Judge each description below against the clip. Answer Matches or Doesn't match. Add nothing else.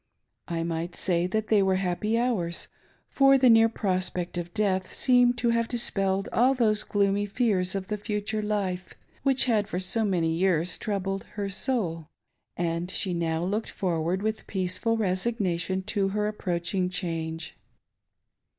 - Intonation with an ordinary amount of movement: Matches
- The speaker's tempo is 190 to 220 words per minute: Doesn't match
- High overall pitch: Matches